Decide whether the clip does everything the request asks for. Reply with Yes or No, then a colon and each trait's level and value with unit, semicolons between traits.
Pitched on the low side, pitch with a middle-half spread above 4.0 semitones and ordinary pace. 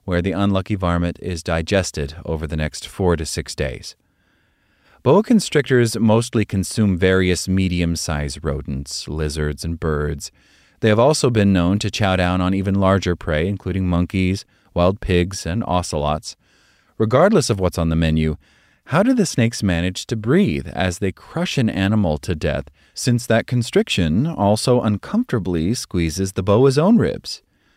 Yes: very low, 95 Hz; average, 5.0 semitones; average, 155 wpm